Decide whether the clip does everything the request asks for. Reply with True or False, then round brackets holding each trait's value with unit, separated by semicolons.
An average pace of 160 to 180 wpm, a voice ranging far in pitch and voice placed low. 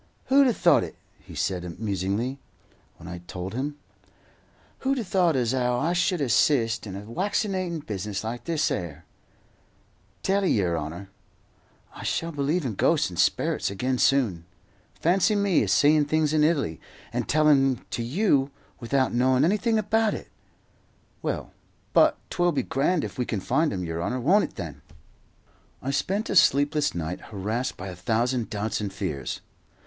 True (170 wpm; 8.6 semitones; 130 Hz)